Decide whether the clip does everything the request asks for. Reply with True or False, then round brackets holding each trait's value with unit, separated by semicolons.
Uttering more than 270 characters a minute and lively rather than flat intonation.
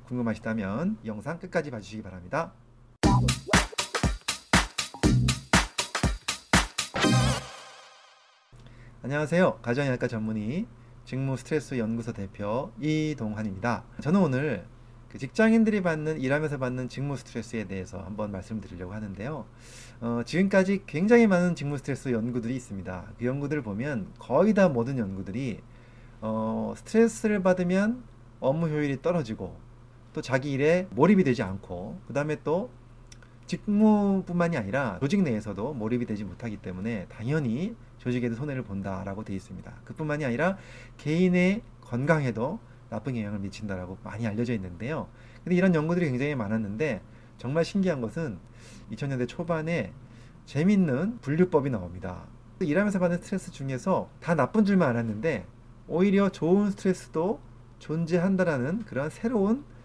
True (325 characters per minute; 6.7 semitones)